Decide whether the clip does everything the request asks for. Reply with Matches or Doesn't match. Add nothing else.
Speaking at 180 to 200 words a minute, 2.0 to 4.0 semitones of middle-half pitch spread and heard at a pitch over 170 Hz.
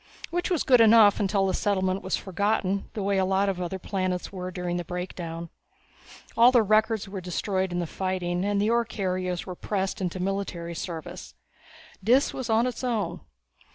Matches